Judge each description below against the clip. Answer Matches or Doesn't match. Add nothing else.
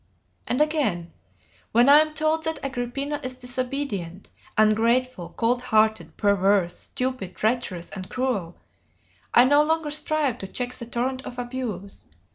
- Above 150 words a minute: Doesn't match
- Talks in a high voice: Matches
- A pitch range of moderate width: Matches